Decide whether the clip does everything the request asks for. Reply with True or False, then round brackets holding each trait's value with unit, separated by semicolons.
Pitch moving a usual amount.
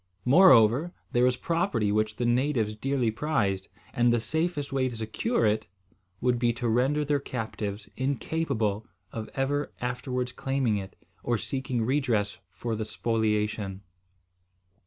True (3.9 semitones)